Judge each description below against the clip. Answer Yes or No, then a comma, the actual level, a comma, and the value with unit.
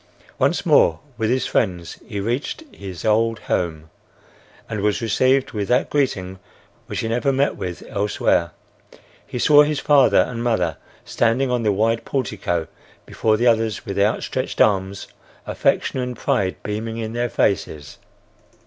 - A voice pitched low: Yes, low, 110 Hz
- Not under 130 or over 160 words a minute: Yes, average, 150 wpm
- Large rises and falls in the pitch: No, average, 3.9 semitones